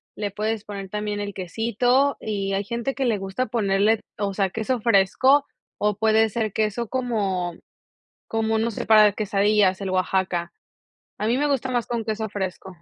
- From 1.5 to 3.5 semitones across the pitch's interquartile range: Yes, average, 2.9 semitones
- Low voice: No, high, 210 Hz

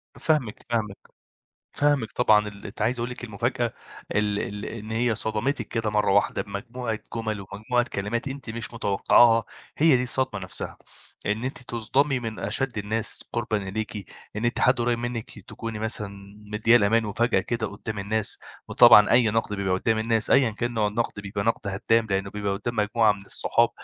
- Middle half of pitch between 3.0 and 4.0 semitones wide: No, narrow, 2.4 semitones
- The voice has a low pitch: Yes, low, 110 Hz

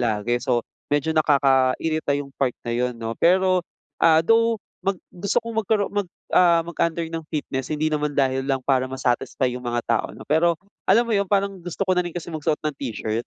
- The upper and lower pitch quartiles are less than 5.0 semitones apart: No, wide, 5.5 semitones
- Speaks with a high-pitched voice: No, medium, 150 Hz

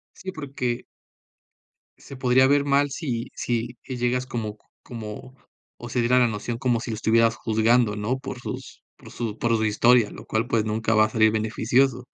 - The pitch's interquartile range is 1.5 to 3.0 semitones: Yes, narrow, 2.4 semitones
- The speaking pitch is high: No, low, 120 Hz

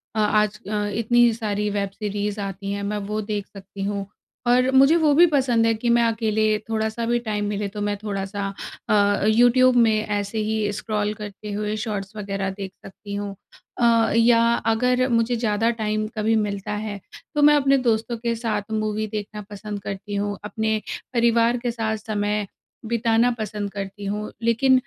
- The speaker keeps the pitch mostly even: Yes, narrow, 2.0 semitones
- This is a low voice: No, high, 215 Hz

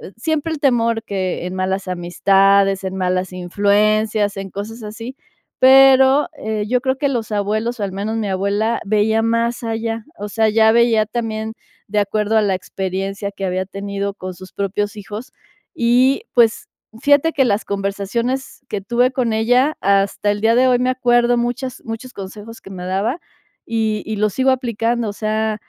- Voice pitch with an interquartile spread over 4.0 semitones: No, average, 3.1 semitones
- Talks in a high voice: Yes, high, 220 Hz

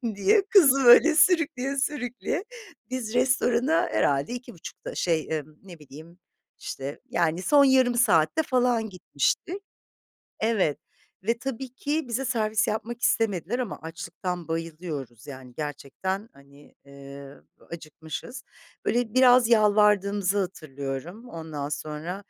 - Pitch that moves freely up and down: Yes, wide, 8.0 semitones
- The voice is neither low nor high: No, high, 205 Hz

